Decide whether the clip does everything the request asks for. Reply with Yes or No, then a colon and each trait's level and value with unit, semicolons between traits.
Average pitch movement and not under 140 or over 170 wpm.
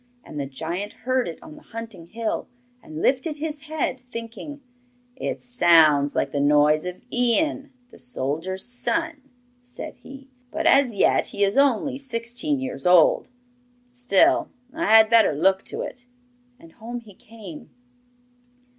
No: wide, 6.8 semitones; average, 145 wpm